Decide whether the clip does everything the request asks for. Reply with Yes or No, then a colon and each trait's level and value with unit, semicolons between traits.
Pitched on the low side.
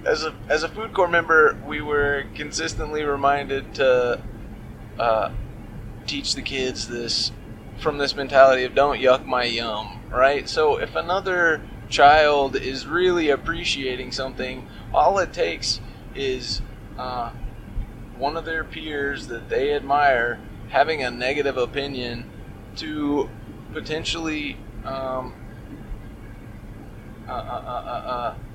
Yes: low, 130 Hz